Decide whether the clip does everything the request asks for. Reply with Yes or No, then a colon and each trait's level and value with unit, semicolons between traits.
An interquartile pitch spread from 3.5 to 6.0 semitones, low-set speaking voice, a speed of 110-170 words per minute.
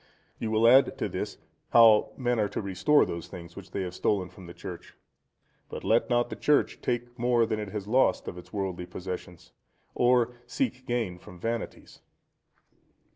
No: average, 4.9 semitones; low, 110 Hz; average, 180 wpm